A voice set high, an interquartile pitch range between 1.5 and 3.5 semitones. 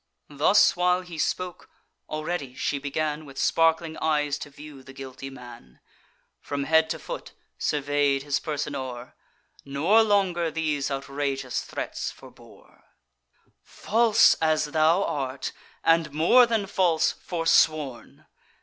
No: medium, 150 Hz; average, 3.2 semitones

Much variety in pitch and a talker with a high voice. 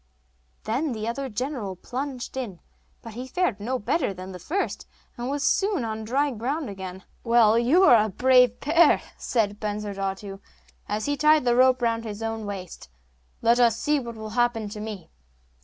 No: average, 3.7 semitones; high, 235 Hz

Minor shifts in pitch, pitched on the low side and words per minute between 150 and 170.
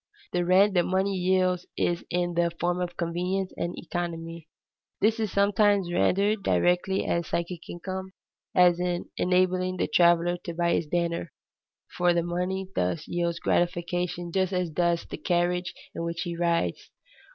No: narrow, 1.3 semitones; medium, 175 Hz; average, 160 wpm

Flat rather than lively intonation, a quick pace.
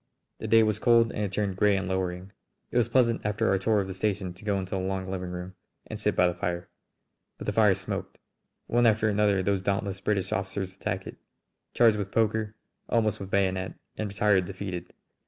Yes: narrow, 2.2 semitones; fast, 210 wpm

